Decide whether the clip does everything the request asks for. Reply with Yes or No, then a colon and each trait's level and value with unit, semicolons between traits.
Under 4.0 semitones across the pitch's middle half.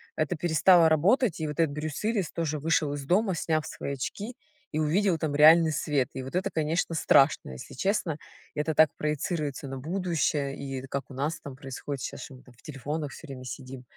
Yes: average, 3.1 semitones